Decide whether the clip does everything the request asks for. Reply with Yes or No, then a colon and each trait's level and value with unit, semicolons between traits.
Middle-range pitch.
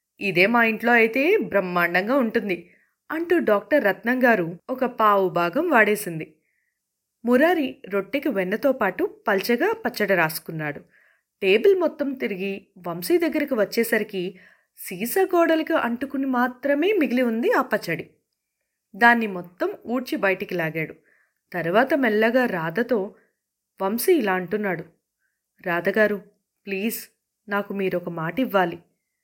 No: high, 225 Hz